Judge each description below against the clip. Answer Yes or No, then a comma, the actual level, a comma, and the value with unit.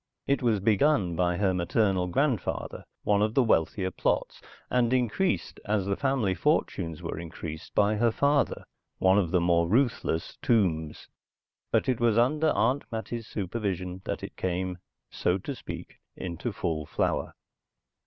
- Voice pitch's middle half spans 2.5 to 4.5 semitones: No, average, 5.0 semitones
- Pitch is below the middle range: Yes, low, 100 Hz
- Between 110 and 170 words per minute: Yes, average, 150 wpm